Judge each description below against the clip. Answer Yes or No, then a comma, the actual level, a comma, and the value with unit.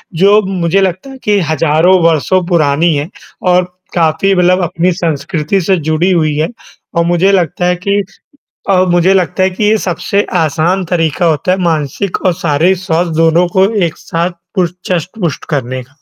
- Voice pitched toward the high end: No, medium, 175 Hz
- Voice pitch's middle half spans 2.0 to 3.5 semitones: Yes, average, 2.7 semitones